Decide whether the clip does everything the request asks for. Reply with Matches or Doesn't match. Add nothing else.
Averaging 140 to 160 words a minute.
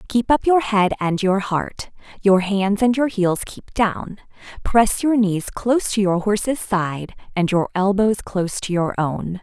Doesn't match